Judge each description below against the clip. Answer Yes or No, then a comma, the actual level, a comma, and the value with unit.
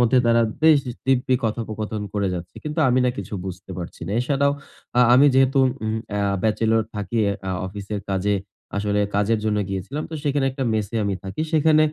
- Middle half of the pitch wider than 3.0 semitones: Yes, average, 4.6 semitones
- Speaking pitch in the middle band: No, low, 110 Hz